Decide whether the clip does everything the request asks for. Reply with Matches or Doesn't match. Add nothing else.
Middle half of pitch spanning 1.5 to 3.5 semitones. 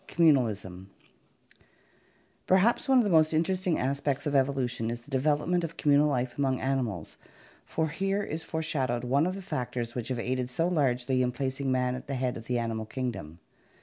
Doesn't match